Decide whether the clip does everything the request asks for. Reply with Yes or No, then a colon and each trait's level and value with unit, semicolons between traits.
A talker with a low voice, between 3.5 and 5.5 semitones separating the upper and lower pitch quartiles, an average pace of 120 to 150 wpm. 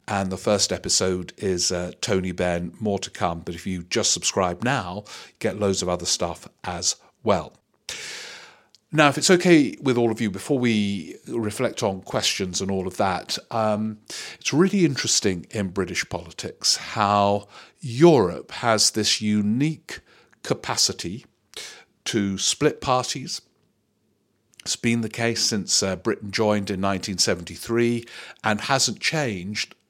Yes: low, 105 Hz; average, 3.8 semitones; average, 140 wpm